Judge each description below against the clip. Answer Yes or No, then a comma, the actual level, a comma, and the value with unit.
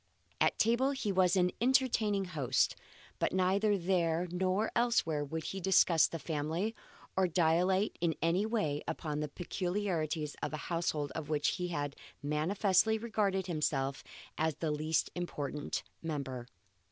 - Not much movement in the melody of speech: No, average, 4.1 semitones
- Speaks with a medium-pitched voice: Yes, medium, 175 Hz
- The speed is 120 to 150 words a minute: Yes, average, 140 wpm